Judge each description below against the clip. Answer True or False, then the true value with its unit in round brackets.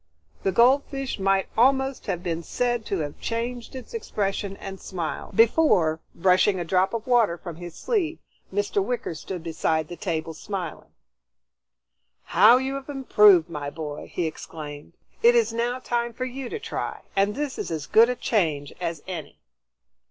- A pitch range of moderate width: False (6.4 semitones)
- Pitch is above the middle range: True (195 Hz)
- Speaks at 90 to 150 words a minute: False (165 wpm)